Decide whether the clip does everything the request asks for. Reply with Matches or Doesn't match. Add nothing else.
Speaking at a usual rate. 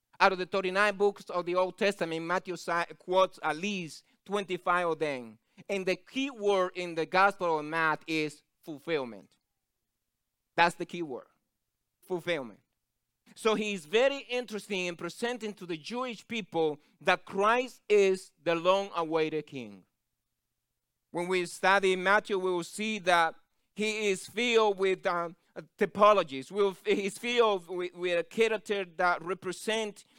Matches